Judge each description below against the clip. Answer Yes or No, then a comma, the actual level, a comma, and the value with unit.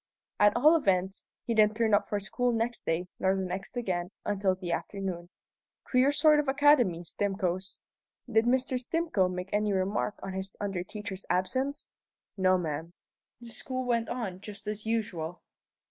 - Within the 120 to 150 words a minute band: No, average, 160 wpm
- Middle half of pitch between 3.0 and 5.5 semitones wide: Yes, average, 4.4 semitones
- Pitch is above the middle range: Yes, high, 205 Hz